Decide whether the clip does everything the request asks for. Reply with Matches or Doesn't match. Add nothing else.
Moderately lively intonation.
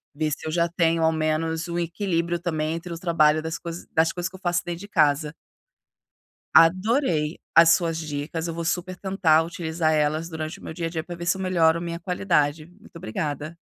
Doesn't match